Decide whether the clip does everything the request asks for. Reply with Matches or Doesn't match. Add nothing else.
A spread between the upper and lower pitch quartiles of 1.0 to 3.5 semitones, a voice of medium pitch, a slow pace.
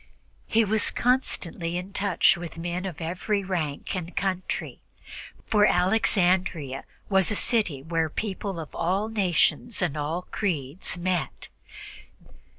Matches